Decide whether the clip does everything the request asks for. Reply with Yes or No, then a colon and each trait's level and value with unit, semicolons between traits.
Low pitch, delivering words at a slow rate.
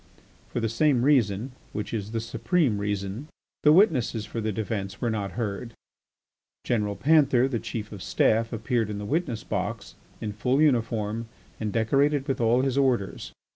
No: low, 115 Hz; average, 170 wpm